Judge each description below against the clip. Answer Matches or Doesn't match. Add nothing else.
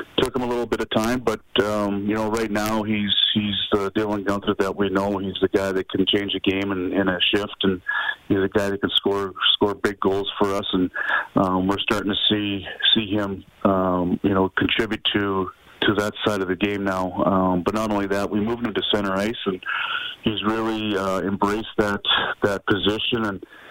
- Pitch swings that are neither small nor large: Doesn't match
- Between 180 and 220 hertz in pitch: Doesn't match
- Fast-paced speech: Matches